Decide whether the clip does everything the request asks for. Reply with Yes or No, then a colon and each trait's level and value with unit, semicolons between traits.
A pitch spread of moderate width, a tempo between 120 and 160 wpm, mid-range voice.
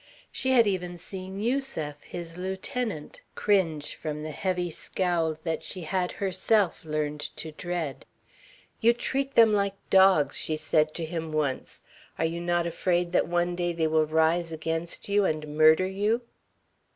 Yes: average, 3.4 semitones; average, 155 wpm; medium, 175 Hz